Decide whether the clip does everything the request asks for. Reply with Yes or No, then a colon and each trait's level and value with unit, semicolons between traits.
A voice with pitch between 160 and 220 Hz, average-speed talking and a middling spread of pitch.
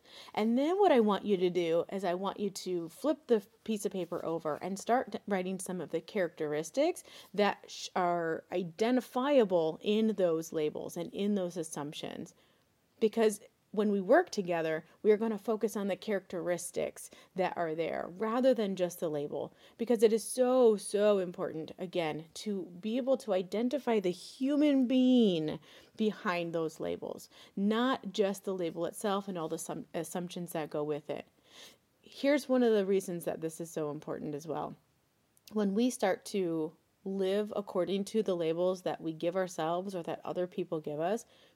Yes: high, 190 Hz; average, 170 wpm; average, 4.6 semitones